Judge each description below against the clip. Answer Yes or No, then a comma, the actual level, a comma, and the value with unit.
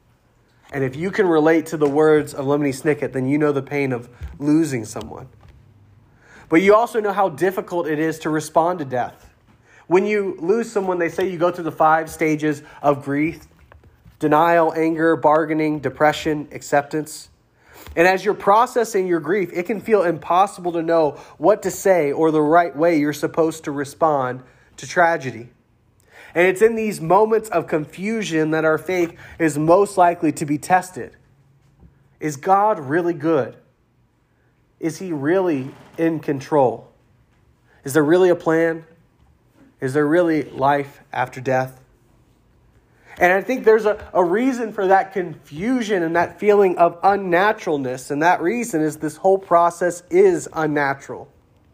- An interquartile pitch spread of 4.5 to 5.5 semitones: No, average, 3.9 semitones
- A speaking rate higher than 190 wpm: No, average, 155 wpm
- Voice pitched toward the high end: No, medium, 160 Hz